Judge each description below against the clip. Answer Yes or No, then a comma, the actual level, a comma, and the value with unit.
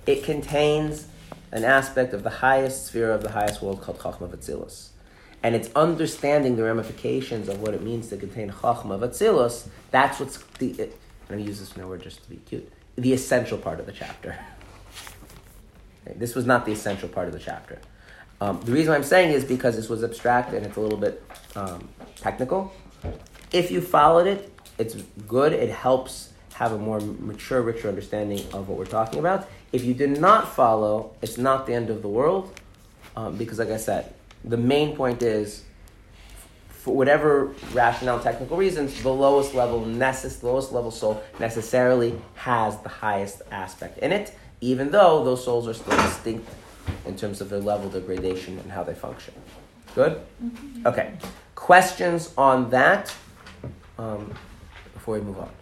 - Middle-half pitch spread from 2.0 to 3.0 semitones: No, average, 4.3 semitones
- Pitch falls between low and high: No, low, 115 Hz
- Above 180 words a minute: No, average, 175 wpm